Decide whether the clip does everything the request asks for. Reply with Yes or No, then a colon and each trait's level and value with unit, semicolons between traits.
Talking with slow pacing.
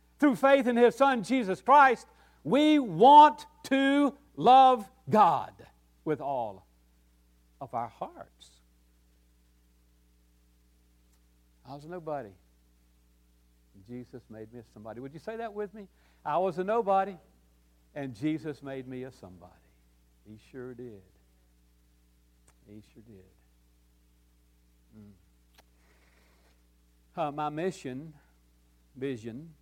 Yes: slow, 110 wpm